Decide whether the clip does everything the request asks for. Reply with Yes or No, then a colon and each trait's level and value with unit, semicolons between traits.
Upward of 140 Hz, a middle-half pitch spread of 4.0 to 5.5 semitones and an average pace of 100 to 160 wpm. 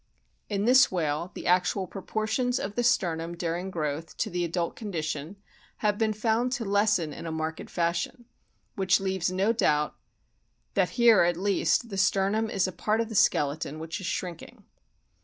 No: high, 190 Hz; average, 4.3 semitones; average, 170 wpm